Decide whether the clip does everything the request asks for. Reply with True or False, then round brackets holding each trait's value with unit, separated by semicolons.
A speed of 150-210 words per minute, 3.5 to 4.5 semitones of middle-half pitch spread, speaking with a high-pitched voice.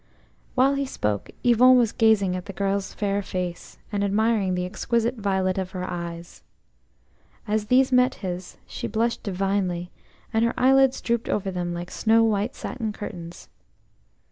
True (155 wpm; 4.1 semitones; 200 Hz)